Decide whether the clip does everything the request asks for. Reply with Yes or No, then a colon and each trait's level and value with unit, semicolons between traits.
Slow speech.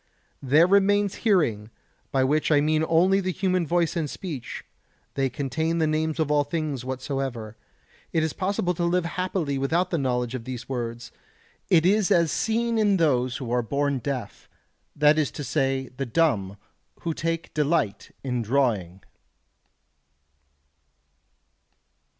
No: average, 145 wpm